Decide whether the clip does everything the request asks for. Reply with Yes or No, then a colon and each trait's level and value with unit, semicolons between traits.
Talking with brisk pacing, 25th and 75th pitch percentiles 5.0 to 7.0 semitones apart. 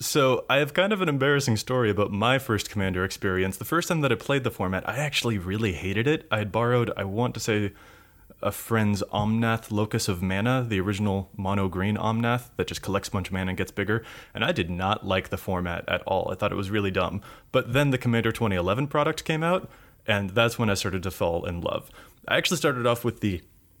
No: fast, 230 wpm; average, 4.0 semitones